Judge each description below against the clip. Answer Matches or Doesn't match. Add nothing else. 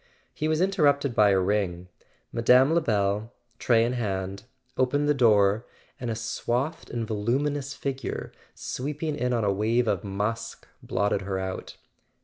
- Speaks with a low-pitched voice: Matches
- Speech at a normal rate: Matches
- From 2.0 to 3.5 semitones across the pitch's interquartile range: Doesn't match